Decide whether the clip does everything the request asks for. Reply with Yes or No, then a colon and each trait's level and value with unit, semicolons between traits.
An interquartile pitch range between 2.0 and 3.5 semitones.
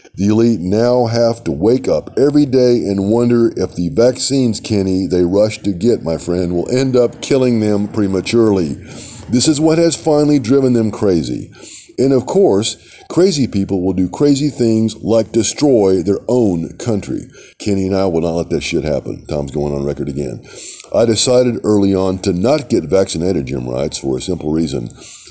No: average, 4.9 semitones